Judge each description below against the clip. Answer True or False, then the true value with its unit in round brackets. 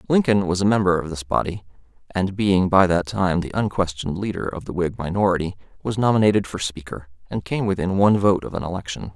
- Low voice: True (95 Hz)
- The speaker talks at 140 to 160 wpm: False (205 wpm)